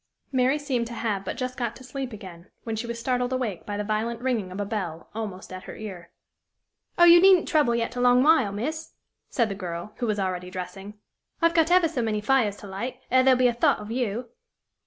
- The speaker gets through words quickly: Yes, fast, 230 wpm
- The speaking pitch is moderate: No, high, 230 Hz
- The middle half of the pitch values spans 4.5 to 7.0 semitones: No, average, 4.1 semitones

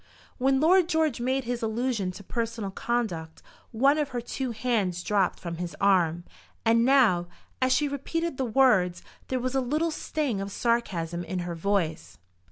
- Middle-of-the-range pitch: No, high, 230 Hz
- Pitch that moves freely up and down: Yes, wide, 6.4 semitones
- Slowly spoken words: No, average, 170 wpm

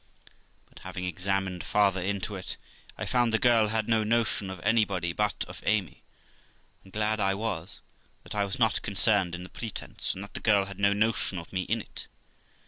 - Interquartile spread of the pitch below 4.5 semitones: Yes, narrow, 2.5 semitones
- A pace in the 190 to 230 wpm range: Yes, average, 195 wpm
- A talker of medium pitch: No, low, 100 Hz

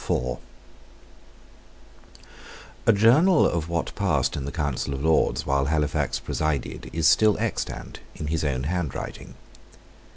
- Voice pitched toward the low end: Yes, very low, 80 Hz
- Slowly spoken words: Yes, slow, 120 wpm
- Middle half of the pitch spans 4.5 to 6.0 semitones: No, average, 3.8 semitones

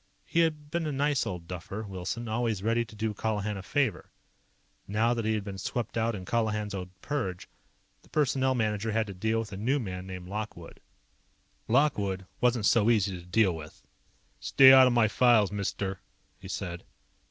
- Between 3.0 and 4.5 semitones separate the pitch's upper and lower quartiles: Yes, average, 3.7 semitones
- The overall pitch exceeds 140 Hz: No, low, 110 Hz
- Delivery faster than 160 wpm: Yes, average, 185 wpm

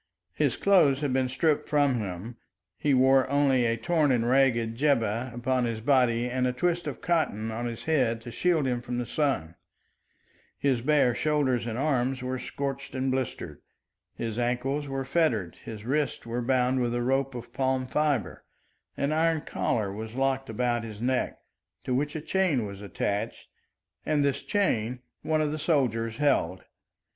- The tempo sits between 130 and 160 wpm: No, average, 170 wpm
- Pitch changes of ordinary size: Yes, average, 3.5 semitones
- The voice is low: Yes, low, 130 Hz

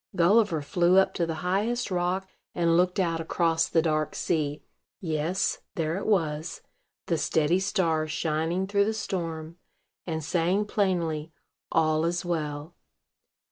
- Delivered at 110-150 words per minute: Yes, average, 140 wpm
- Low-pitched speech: No, medium, 170 Hz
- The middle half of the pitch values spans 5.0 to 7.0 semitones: No, average, 2.9 semitones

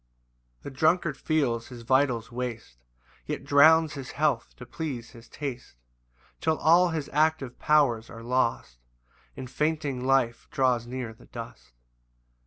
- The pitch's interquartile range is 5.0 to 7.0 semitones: No, average, 4.4 semitones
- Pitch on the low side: Yes, low, 130 Hz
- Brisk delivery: No, average, 140 wpm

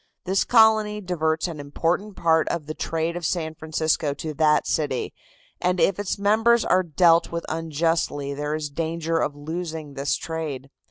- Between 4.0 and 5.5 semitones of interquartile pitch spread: No, average, 2.7 semitones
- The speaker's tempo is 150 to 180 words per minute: Yes, average, 165 wpm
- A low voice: No, medium, 165 Hz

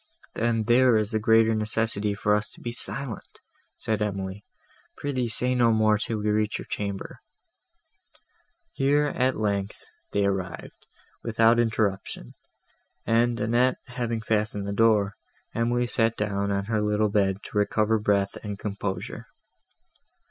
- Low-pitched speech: Yes, low, 110 Hz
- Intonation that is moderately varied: No, narrow, 2.3 semitones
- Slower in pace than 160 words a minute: Yes, average, 140 wpm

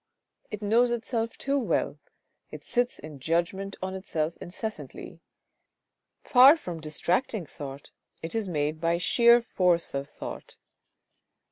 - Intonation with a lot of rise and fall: Yes, wide, 6.4 semitones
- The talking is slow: Yes, slow, 125 wpm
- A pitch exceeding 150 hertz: Yes, medium, 185 Hz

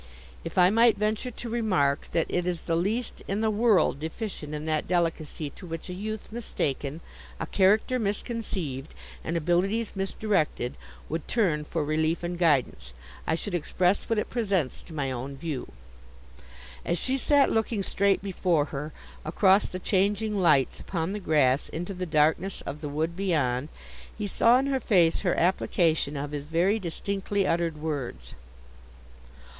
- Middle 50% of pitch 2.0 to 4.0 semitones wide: No, average, 5.0 semitones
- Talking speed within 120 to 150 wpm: No, average, 160 wpm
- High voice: No, medium, 175 Hz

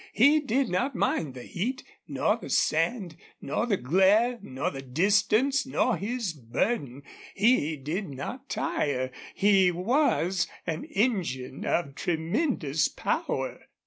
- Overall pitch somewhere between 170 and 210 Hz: Yes, high, 190 Hz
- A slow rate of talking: Yes, slow, 125 wpm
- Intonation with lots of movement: Yes, wide, 8.5 semitones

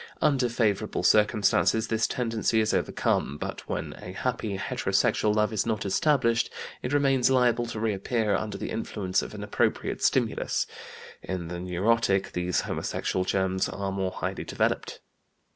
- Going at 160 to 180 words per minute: No, average, 145 wpm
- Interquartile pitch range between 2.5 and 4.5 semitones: Yes, average, 3.4 semitones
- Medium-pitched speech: No, low, 105 Hz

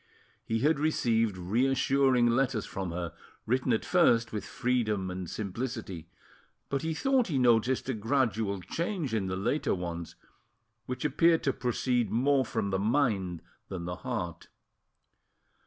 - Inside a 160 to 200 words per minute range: No, average, 140 wpm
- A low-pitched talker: Yes, low, 115 Hz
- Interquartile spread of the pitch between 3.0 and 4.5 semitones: No, wide, 5.6 semitones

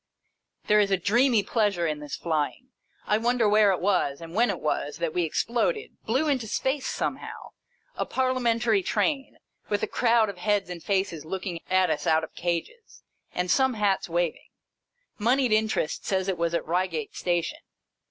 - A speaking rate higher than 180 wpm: No, average, 170 wpm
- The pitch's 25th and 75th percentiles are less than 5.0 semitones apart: No, wide, 5.4 semitones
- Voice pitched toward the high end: Yes, high, 200 Hz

